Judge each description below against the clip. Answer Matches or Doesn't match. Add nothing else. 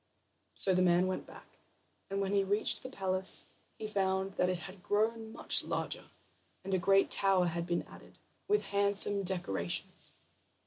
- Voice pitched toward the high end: Matches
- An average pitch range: Doesn't match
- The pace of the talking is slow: Doesn't match